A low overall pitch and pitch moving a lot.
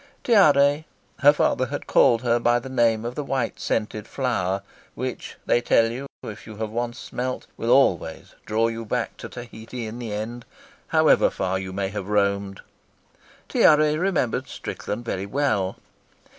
No: low, 115 Hz; average, 3.7 semitones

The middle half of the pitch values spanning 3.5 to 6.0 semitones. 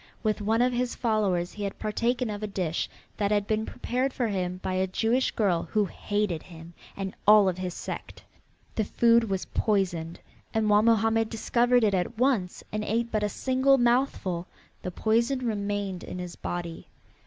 Yes: average, 3.8 semitones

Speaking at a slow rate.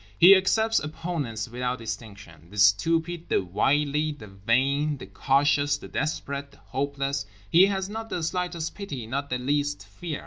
No: average, 150 wpm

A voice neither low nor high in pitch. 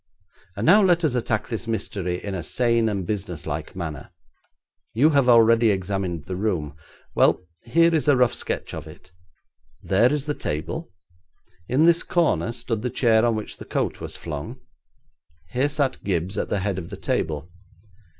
No: low, 110 Hz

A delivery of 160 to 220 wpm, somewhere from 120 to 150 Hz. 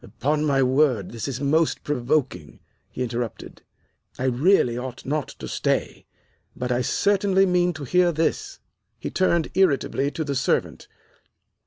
No: average, 145 wpm; medium, 140 Hz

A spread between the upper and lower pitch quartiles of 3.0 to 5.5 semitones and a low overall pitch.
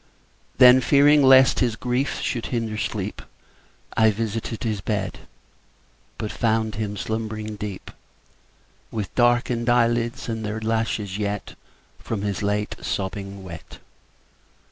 No: narrow, 2.5 semitones; low, 110 Hz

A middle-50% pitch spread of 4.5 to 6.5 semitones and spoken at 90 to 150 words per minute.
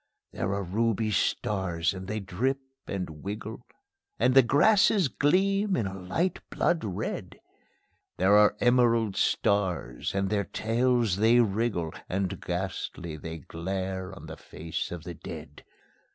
Yes: average, 4.8 semitones; average, 140 wpm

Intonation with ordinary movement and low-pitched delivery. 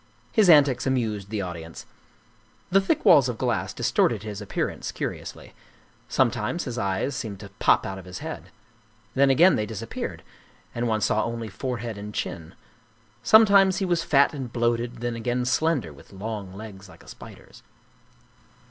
Yes: average, 5.0 semitones; low, 115 Hz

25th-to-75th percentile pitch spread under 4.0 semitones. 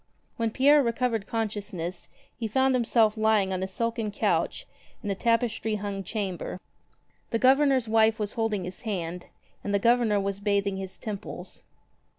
Yes: average, 2.8 semitones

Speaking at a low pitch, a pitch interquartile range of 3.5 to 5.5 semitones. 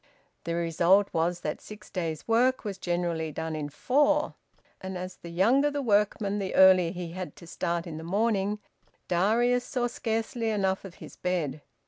No: high, 190 Hz; average, 4.6 semitones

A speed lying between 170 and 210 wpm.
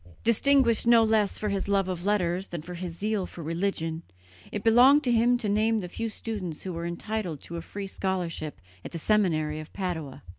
Yes: average, 200 wpm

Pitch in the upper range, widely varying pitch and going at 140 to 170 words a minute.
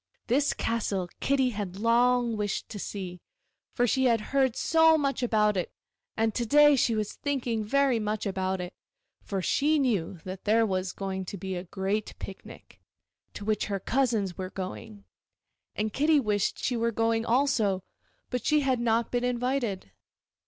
No: high, 225 Hz; average, 4.2 semitones; average, 165 wpm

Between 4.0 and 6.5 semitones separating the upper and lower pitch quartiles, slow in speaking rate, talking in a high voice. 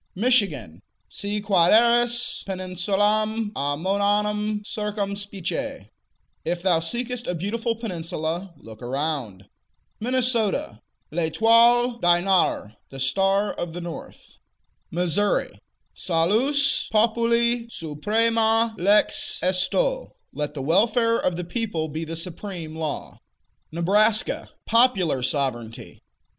Yes: wide, 5.6 semitones; slow, 95 wpm; high, 200 Hz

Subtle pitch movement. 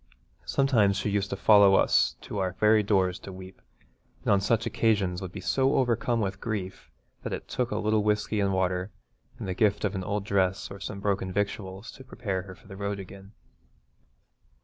Yes: narrow, 2.0 semitones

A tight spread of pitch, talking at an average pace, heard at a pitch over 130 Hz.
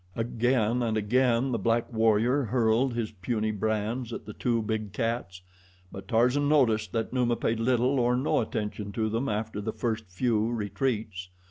No: narrow, 2.3 semitones; average, 165 wpm; low, 115 Hz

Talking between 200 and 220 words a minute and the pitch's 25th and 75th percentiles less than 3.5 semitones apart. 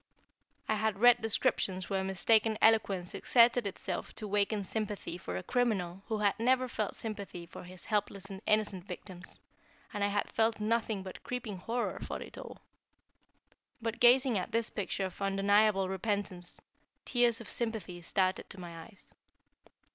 No: average, 155 wpm; average, 2.9 semitones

